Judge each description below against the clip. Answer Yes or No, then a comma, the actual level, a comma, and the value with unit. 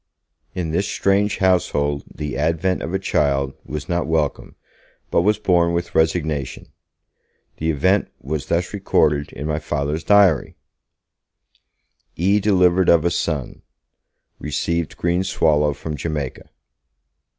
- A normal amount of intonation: Yes, average, 3.5 semitones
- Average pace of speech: No, slow, 125 wpm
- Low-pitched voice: Yes, very low, 80 Hz